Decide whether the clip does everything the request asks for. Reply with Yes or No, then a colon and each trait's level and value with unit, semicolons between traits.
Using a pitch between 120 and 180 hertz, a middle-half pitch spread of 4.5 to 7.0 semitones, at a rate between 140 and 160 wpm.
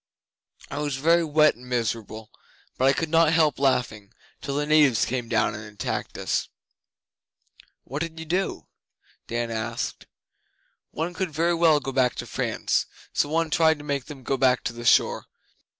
No: medium, 140 Hz; average, 4.8 semitones; average, 170 wpm